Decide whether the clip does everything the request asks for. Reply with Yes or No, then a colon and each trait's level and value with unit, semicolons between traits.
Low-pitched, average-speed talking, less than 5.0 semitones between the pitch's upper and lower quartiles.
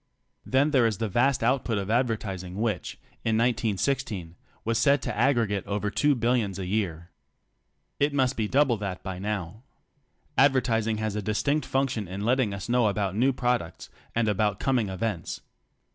Yes: low, 110 Hz; average, 165 wpm; average, 3.9 semitones